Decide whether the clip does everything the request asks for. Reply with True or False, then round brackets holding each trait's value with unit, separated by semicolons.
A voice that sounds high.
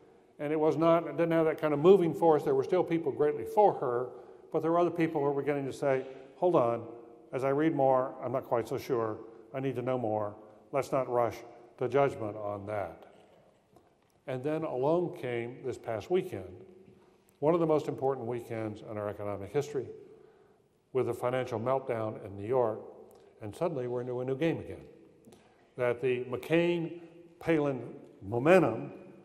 False (135 Hz)